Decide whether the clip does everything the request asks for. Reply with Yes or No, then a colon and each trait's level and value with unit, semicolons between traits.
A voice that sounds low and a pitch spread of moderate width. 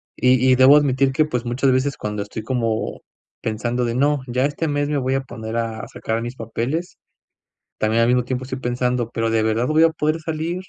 Yes: low, 125 Hz; average, 3.6 semitones